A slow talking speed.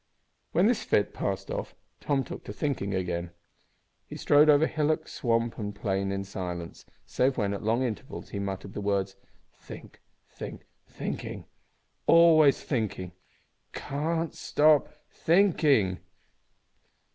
Yes: slow, 130 wpm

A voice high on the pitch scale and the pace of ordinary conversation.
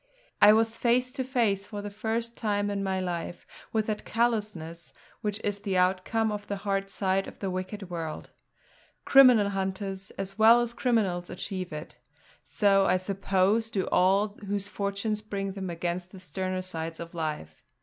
Yes: high, 195 Hz; average, 170 wpm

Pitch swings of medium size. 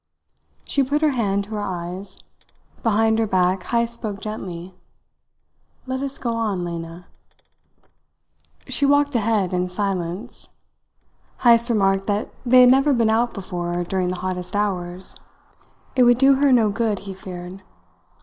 Yes: average, 4.5 semitones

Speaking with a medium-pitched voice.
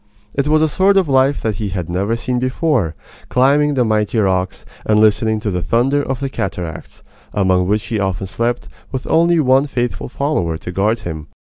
No: low, 115 Hz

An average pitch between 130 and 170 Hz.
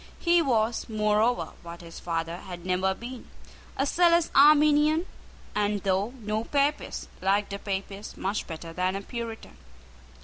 No: high, 210 Hz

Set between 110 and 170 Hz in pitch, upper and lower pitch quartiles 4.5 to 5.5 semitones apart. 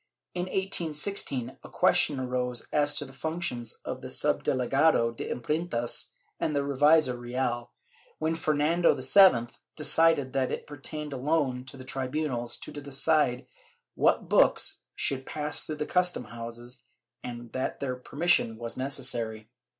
No: low, 135 Hz; average, 3.8 semitones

